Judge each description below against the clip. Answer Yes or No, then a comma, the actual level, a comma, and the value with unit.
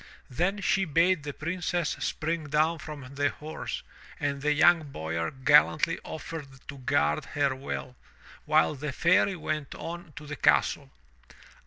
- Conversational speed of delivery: Yes, average, 145 wpm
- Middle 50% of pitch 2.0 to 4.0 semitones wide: Yes, average, 3.1 semitones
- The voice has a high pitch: No, medium, 150 Hz